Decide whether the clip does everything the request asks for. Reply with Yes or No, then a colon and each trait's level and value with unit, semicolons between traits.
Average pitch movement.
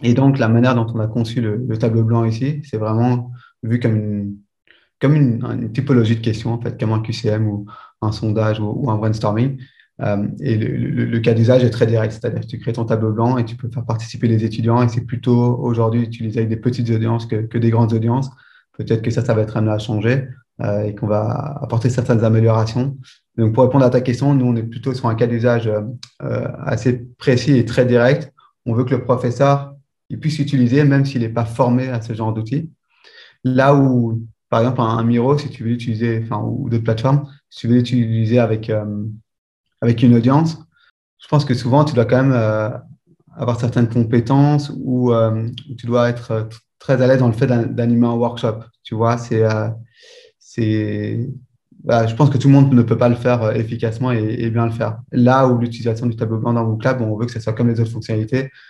No: narrow, 2.1 semitones